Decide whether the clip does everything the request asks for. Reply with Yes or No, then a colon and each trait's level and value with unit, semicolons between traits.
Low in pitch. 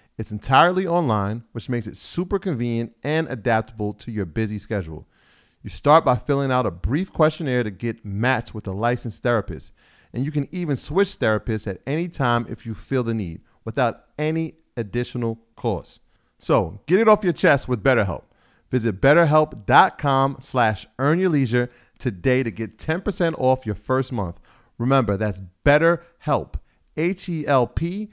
Yes: low, 125 Hz